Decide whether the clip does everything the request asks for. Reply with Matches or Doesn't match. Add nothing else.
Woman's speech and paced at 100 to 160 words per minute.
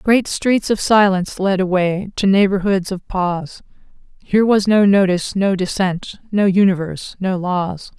Matches